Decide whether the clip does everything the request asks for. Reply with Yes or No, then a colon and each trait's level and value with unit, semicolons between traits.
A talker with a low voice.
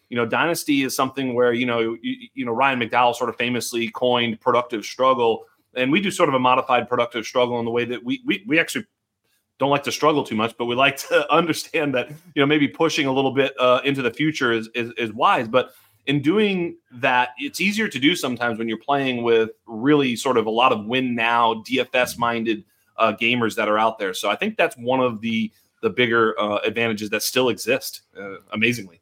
Yes: low, 125 Hz